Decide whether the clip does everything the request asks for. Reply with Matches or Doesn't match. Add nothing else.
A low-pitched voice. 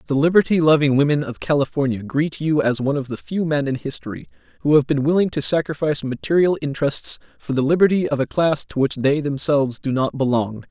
Doesn't match